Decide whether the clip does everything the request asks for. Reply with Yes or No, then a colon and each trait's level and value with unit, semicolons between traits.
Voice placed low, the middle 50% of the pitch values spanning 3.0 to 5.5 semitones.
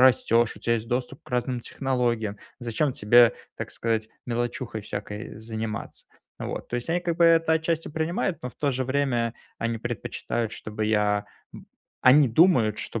Yes: low, 120 Hz; average, 3.5 semitones